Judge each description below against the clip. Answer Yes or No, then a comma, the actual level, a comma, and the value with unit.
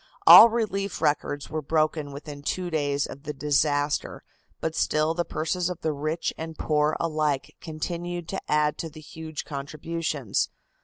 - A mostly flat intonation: Yes, narrow, 2.1 semitones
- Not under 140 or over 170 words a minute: Yes, average, 155 wpm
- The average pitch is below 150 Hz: No, medium, 155 Hz